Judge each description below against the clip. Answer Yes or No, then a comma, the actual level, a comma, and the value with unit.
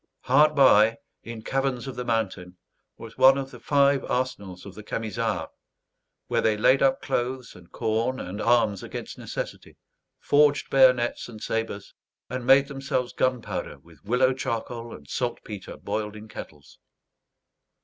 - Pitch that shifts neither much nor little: Yes, average, 3.6 semitones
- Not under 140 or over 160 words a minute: Yes, average, 145 wpm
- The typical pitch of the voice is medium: No, low, 120 Hz